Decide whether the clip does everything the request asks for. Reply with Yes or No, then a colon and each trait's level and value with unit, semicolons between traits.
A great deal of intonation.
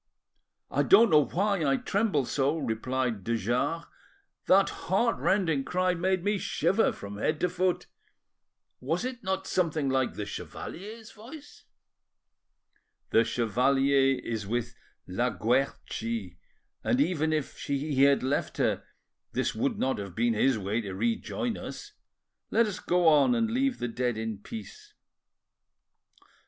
Yes: wide, 8.1 semitones